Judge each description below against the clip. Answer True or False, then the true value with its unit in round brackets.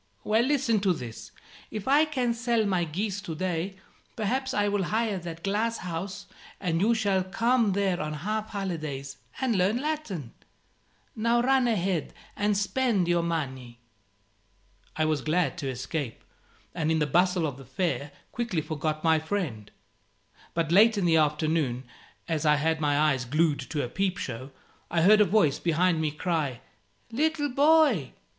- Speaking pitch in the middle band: True (180 Hz)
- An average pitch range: False (5.9 semitones)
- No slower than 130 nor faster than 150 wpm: False (165 wpm)